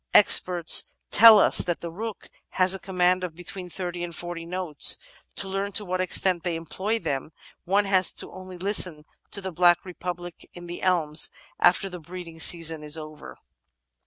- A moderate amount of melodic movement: No, narrow, 2.0 semitones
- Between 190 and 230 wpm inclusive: No, average, 175 wpm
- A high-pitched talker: No, medium, 180 Hz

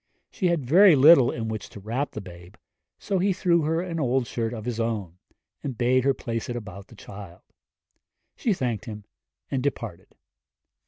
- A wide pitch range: Yes, wide, 5.7 semitones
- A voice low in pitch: Yes, low, 120 Hz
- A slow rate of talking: No, average, 180 wpm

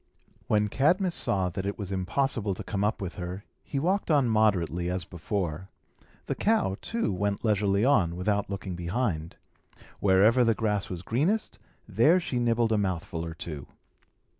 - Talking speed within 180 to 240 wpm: No, average, 165 wpm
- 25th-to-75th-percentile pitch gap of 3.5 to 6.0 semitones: Yes, average, 4.7 semitones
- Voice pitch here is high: No, low, 100 Hz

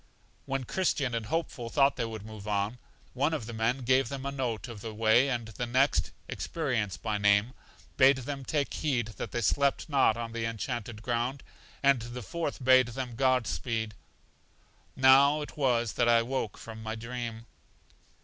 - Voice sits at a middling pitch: No, low, 120 Hz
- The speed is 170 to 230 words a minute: Yes, average, 180 wpm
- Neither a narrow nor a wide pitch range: Yes, average, 3.1 semitones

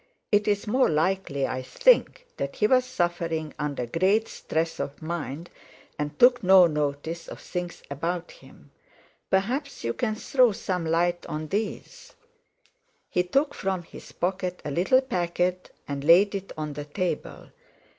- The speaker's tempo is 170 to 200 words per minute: No, average, 145 wpm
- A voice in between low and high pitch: Yes, medium, 175 Hz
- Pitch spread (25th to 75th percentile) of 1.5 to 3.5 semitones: No, average, 4.7 semitones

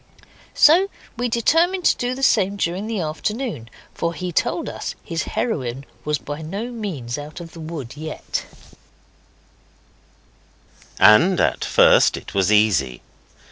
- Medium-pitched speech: Yes, medium, 170 Hz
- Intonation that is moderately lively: No, wide, 7.9 semitones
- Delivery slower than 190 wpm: Yes, average, 140 wpm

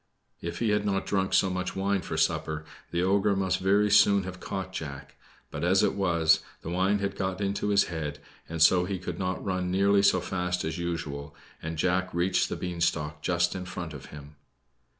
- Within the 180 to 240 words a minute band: Yes, average, 200 wpm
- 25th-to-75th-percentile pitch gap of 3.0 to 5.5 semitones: No, narrow, 2.5 semitones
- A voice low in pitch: Yes, very low, 90 Hz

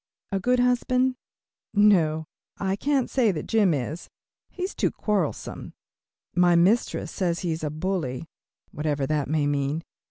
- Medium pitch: Yes, medium, 175 Hz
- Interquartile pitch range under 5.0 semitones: No, wide, 5.6 semitones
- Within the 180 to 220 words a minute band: No, average, 150 wpm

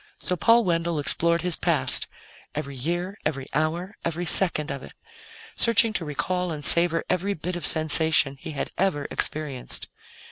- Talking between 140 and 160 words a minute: Yes, average, 155 wpm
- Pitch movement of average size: Yes, average, 3.2 semitones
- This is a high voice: No, medium, 165 Hz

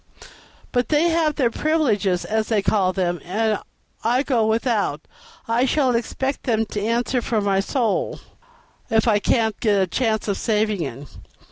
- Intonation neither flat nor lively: Yes, average, 3.6 semitones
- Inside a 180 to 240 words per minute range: No, average, 160 wpm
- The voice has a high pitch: Yes, high, 220 Hz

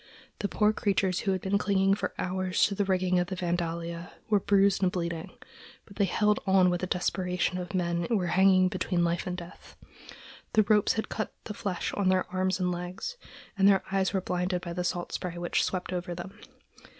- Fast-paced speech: Yes, fast, 210 wpm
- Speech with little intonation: Yes, narrow, 1.7 semitones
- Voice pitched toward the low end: No, medium, 185 Hz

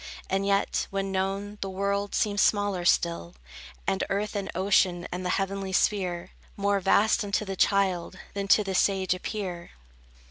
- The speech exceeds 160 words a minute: No, average, 155 wpm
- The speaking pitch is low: No, high, 195 Hz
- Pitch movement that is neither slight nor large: No, narrow, 1.5 semitones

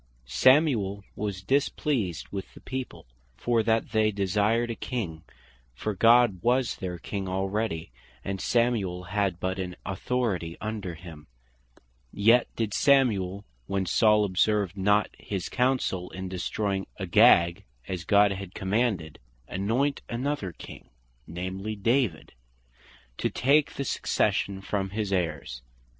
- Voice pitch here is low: Yes, low, 100 Hz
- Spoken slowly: Yes, slow, 125 wpm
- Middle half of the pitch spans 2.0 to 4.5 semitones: Yes, average, 3.8 semitones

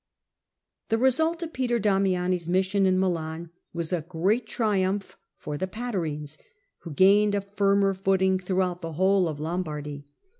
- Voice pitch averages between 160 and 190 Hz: Yes, medium, 185 Hz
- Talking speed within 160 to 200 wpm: No, average, 145 wpm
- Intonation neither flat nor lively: Yes, average, 3.0 semitones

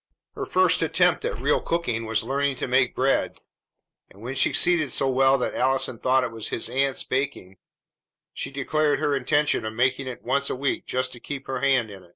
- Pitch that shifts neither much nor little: No, narrow, 2.1 semitones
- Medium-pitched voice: No, low, 130 Hz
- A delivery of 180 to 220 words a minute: Yes, average, 200 wpm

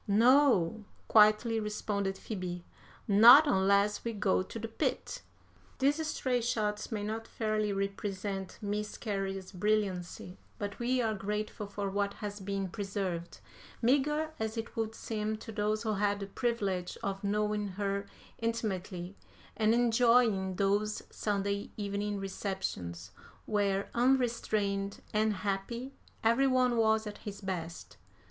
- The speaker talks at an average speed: No, slow, 130 wpm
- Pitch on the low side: No, high, 210 Hz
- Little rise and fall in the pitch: Yes, narrow, 2.3 semitones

